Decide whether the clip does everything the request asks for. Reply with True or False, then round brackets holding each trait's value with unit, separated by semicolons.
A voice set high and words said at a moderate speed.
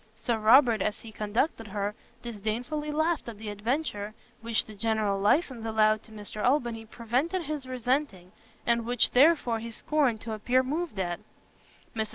True (230 Hz; 160 wpm)